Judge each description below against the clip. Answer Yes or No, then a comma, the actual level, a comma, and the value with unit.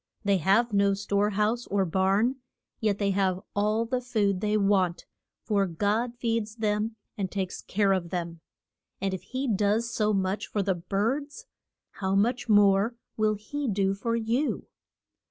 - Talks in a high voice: Yes, high, 205 Hz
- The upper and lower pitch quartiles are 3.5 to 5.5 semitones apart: No, narrow, 2.6 semitones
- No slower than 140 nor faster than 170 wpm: Yes, average, 160 wpm